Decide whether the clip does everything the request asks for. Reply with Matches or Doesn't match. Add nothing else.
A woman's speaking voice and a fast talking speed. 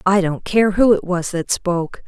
Matches